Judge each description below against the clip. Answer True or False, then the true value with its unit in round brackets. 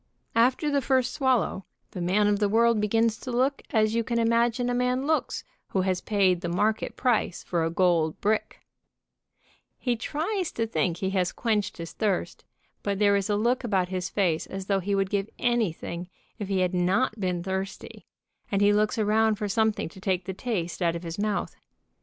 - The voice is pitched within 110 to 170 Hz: False (205 Hz)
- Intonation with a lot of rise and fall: False (3.8 semitones)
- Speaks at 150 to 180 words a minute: False (195 wpm)